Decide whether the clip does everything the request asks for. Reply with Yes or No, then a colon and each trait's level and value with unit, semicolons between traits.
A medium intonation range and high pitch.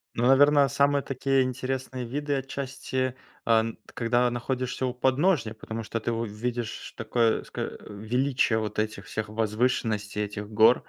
No: average, 3.1 semitones; low, 120 Hz